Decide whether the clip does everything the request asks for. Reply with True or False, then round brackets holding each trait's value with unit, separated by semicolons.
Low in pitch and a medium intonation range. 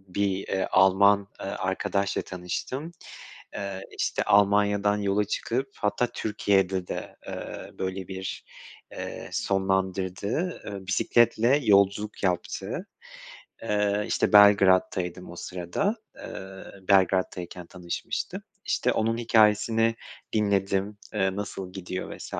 False (100 Hz; 1.8 semitones)